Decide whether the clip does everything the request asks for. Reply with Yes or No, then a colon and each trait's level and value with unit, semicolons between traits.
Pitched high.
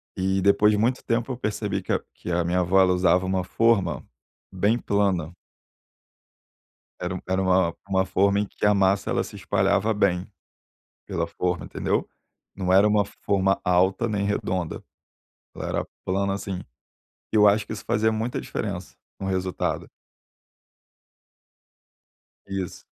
No: very low, 95 Hz